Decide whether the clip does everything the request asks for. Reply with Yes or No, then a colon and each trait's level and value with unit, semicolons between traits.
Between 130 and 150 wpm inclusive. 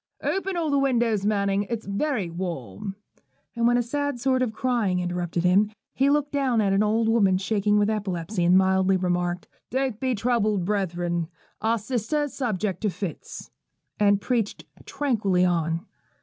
No: average, 165 wpm